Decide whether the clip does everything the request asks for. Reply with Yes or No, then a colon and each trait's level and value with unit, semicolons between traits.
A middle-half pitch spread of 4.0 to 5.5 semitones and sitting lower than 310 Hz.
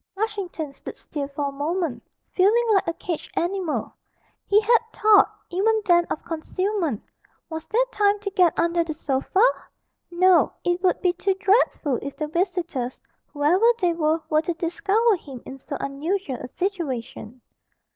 No: average, 4.8 semitones; very high, 345 Hz